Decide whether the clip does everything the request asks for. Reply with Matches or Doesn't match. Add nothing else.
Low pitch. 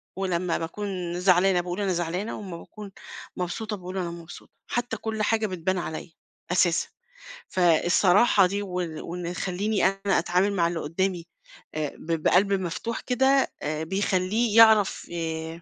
Doesn't match